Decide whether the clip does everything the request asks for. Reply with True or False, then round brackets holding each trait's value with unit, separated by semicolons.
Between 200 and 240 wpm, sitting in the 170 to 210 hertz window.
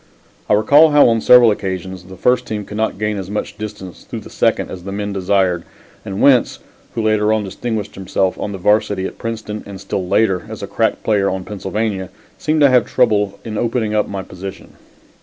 False (205 wpm; 105 Hz)